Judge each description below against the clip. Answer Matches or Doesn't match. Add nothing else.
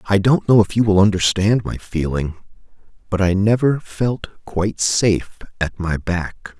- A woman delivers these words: Doesn't match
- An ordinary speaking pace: Matches